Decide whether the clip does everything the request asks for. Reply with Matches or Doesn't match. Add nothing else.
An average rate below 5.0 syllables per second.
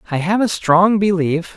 Matches